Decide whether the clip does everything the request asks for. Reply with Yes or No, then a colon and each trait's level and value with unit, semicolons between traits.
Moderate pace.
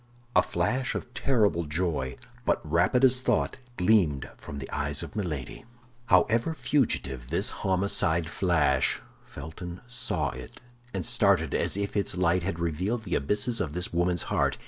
Yes: average, 150 wpm